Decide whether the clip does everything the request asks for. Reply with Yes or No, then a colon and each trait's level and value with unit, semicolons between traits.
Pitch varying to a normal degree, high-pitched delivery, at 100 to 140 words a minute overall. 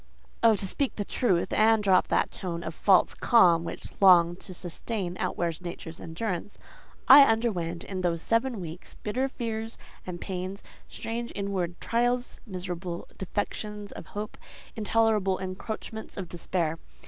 Yes: average, 4.2 semitones; high, 195 Hz; slow, 135 wpm